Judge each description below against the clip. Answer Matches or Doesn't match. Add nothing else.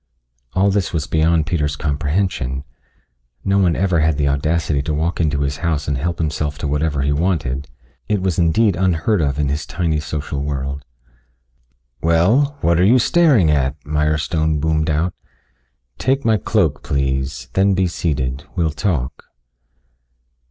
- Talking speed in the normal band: Matches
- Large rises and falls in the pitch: Doesn't match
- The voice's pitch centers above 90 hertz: Doesn't match